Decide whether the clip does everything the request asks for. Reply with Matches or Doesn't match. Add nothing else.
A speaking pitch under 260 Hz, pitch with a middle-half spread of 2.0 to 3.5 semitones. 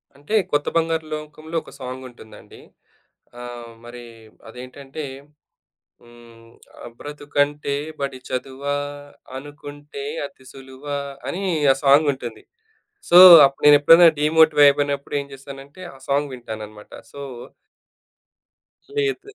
Matches